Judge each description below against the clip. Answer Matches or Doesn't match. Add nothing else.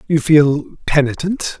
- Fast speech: Doesn't match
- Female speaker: Doesn't match